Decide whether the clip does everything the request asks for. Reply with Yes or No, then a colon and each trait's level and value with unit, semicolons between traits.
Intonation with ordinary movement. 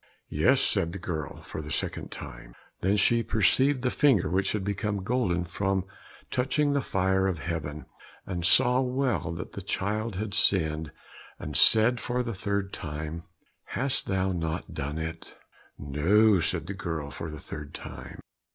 Yes: average, 5.0 semitones